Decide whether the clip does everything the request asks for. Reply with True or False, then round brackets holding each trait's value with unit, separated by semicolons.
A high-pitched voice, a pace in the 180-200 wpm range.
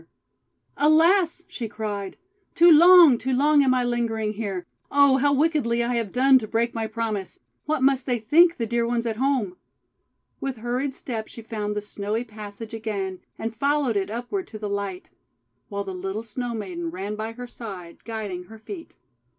True (230 Hz; 190 wpm)